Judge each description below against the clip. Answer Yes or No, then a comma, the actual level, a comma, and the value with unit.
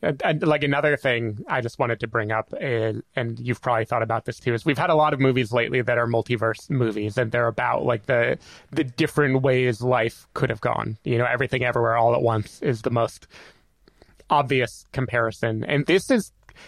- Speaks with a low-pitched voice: Yes, low, 125 Hz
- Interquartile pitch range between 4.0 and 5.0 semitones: No, average, 2.9 semitones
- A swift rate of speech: Yes, fast, 210 wpm